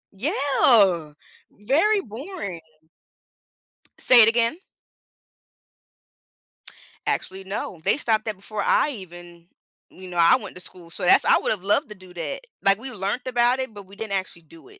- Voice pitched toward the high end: Yes, high, 205 Hz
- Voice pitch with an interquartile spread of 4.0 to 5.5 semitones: Yes, average, 5.1 semitones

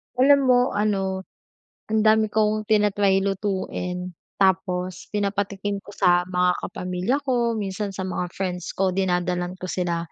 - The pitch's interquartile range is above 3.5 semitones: No, narrow, 2.5 semitones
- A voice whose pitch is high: Yes, high, 195 Hz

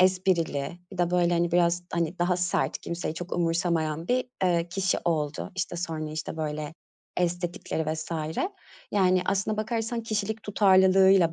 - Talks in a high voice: No, medium, 175 Hz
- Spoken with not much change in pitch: Yes, narrow, 2.3 semitones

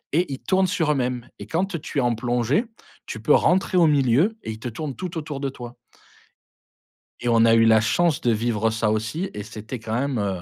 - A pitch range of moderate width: No, wide, 5.8 semitones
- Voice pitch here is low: Yes, low, 125 Hz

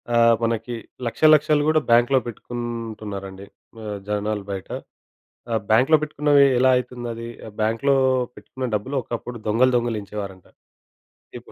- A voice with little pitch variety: No, average, 3.2 semitones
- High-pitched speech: No, low, 115 Hz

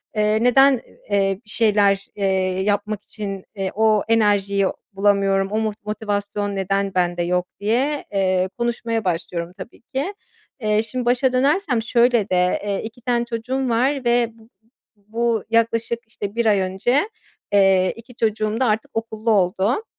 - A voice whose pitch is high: Yes, high, 215 Hz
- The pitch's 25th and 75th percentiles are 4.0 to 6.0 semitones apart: No, average, 3.2 semitones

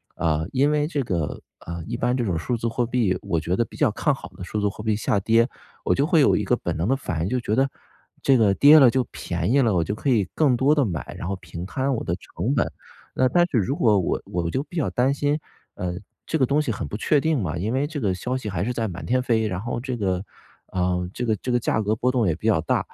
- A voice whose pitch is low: Yes, low, 115 Hz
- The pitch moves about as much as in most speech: No, wide, 6.1 semitones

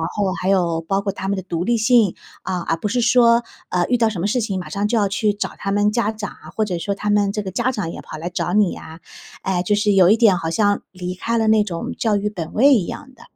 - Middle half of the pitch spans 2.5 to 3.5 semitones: Yes, average, 3.1 semitones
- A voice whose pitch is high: Yes, high, 205 Hz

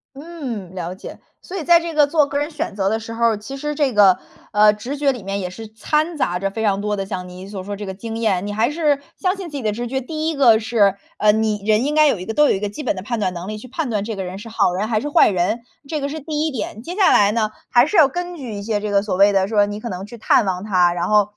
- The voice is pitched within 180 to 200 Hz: No, high, 220 Hz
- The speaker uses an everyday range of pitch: No, wide, 6.1 semitones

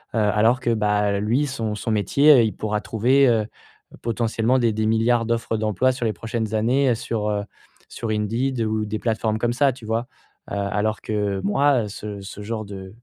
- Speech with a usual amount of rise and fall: No, narrow, 2.1 semitones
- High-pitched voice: No, low, 110 Hz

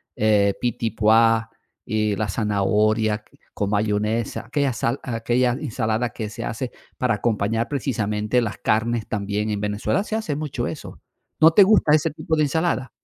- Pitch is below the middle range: Yes, low, 115 Hz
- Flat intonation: No, average, 3.5 semitones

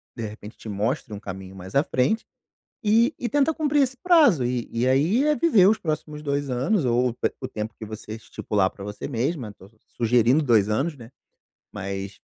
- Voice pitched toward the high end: No, low, 125 Hz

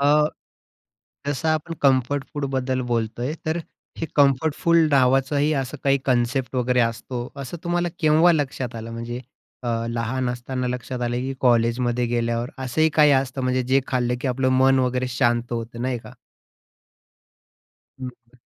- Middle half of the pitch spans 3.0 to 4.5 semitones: No, narrow, 2.6 semitones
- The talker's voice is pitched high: No, low, 130 Hz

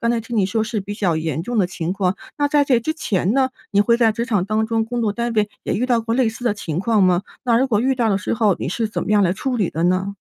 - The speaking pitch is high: Yes, high, 220 Hz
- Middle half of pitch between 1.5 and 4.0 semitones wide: Yes, average, 3.5 semitones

